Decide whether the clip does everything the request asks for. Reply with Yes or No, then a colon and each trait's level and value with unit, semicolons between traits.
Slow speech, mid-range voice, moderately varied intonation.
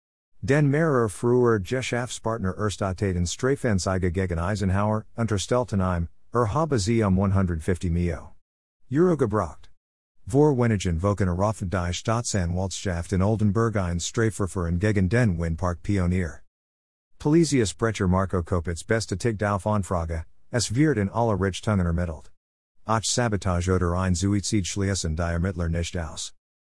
No: slow, 125 wpm; low, 100 Hz; average, 4.3 semitones